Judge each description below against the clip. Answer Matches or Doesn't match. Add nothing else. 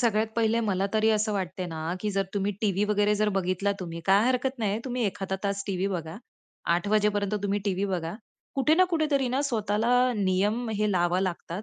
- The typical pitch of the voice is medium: Doesn't match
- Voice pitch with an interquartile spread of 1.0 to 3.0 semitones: Matches